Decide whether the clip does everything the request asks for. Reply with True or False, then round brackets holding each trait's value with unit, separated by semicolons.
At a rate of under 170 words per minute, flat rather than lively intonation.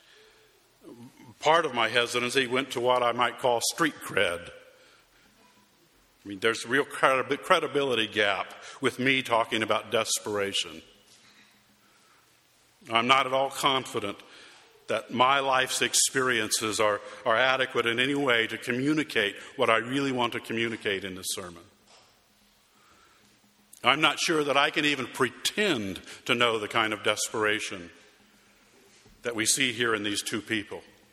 False (140 wpm; 3.4 semitones)